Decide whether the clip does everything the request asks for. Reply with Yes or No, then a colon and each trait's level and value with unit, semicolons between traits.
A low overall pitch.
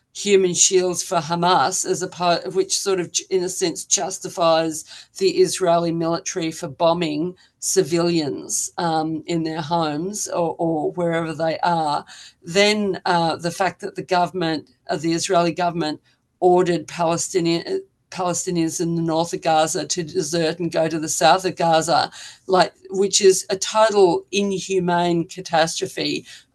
No: medium, 175 Hz